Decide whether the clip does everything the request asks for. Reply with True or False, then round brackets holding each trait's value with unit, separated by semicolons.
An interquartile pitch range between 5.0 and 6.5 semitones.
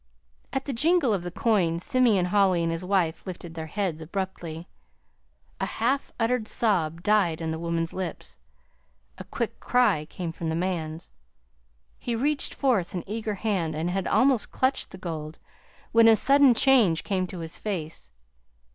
True (5.4 semitones)